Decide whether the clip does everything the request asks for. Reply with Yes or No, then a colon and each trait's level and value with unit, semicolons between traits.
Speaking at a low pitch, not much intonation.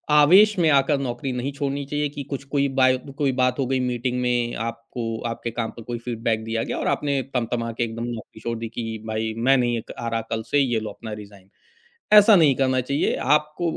No: low, 125 Hz; average, 3.2 semitones